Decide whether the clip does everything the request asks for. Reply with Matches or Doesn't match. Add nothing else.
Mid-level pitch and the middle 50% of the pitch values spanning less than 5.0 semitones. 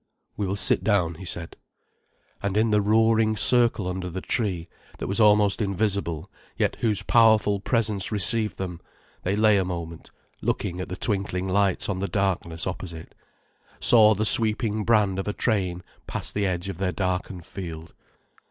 Doesn't match